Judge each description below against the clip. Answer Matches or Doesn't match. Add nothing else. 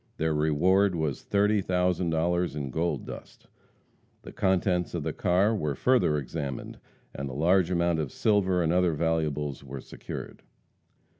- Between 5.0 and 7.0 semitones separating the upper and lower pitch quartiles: Doesn't match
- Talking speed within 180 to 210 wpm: Doesn't match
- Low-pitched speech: Matches